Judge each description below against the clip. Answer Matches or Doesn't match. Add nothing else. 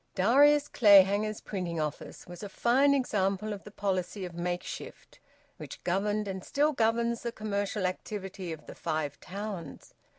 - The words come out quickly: Doesn't match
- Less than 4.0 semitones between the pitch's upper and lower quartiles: Matches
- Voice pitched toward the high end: Matches